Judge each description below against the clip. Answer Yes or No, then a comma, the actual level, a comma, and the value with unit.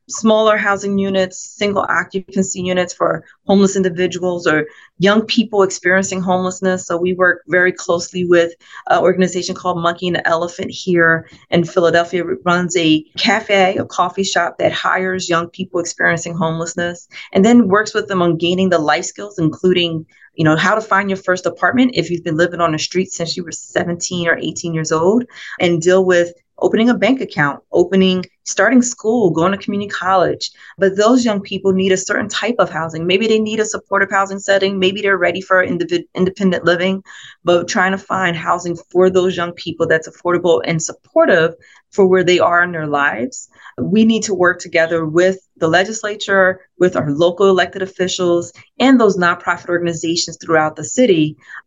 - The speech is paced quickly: No, average, 180 wpm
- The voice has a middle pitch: Yes, medium, 180 Hz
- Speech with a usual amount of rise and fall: No, narrow, 2.1 semitones